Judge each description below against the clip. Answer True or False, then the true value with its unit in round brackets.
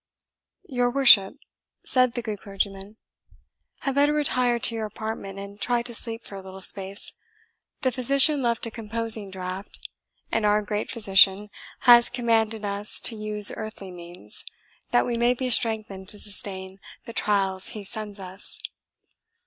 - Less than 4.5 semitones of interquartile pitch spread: True (3.2 semitones)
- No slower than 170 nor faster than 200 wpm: False (150 wpm)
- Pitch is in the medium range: False (215 Hz)